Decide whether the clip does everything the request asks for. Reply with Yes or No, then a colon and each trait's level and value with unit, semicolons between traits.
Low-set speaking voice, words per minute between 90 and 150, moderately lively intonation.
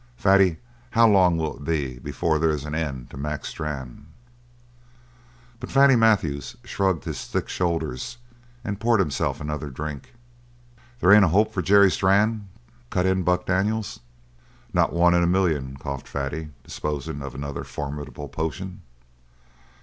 Yes: very low, 80 Hz; average, 145 wpm; average, 5.0 semitones